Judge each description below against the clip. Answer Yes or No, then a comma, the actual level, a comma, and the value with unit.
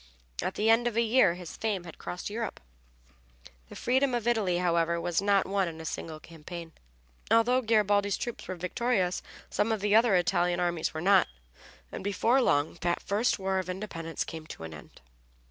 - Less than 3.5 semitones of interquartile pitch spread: No, average, 4.4 semitones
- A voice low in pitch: No, high, 190 Hz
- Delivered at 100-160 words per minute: No, average, 185 wpm